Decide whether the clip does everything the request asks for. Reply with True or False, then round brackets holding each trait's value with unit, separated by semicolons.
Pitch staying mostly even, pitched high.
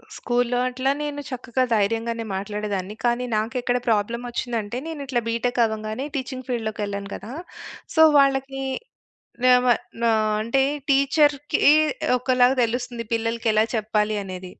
False (3.0 semitones; 240 Hz)